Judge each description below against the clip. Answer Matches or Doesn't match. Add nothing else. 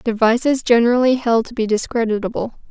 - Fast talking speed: Doesn't match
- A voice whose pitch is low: Doesn't match